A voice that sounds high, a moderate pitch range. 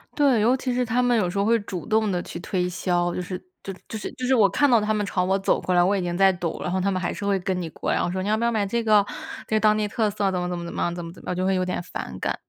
Yes: high, 195 Hz; average, 3.2 semitones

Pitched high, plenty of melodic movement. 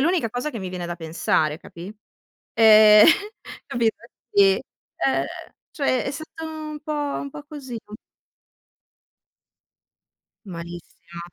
Yes: high, 220 Hz; wide, 8.7 semitones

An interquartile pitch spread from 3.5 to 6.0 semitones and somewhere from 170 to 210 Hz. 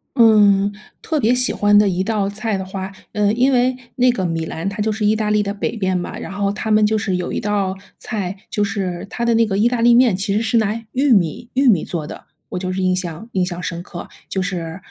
No: average, 3.0 semitones; high, 205 Hz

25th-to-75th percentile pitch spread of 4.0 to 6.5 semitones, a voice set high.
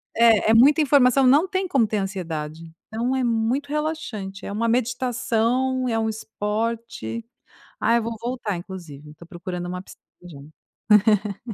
Yes: average, 4.5 semitones; high, 230 Hz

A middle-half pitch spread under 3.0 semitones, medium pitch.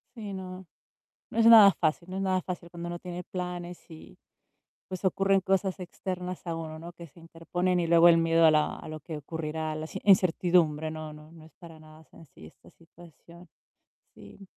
Yes: narrow, 2.4 semitones; medium, 170 Hz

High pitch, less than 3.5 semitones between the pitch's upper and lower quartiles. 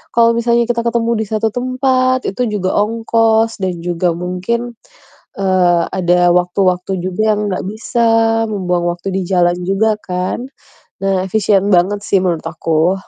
No: high, 195 Hz; average, 4.2 semitones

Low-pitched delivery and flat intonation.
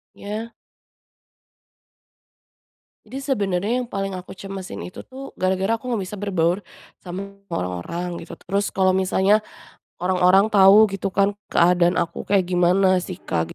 No: high, 190 Hz; narrow, 2.2 semitones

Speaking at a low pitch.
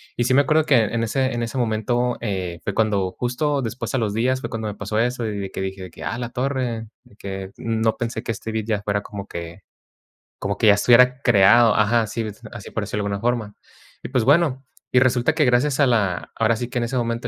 Yes: low, 115 Hz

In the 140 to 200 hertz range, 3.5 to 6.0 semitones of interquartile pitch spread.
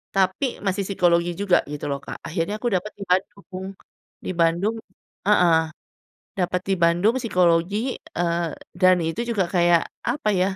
No: medium, 185 Hz; average, 3.0 semitones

